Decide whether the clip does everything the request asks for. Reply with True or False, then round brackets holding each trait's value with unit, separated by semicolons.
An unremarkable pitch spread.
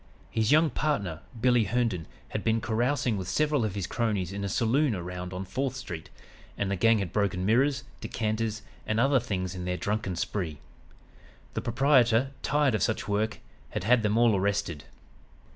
True (4.5 semitones)